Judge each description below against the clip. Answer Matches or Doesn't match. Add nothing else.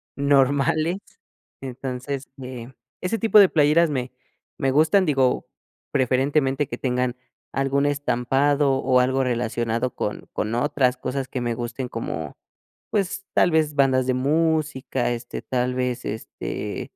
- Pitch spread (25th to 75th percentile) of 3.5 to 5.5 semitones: Doesn't match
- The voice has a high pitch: Doesn't match